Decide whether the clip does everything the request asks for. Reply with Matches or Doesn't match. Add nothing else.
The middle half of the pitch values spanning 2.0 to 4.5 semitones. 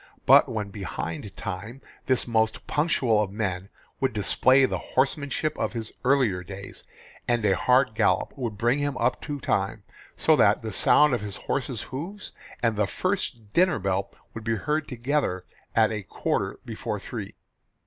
Doesn't match